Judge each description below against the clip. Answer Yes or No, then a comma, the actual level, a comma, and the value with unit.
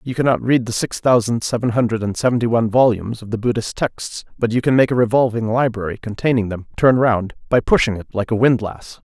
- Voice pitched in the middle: No, low, 115 Hz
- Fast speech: Yes, fast, 215 wpm